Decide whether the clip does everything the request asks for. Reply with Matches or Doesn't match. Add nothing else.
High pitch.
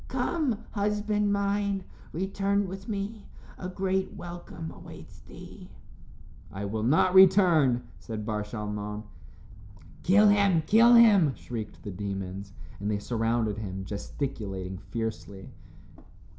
Doesn't match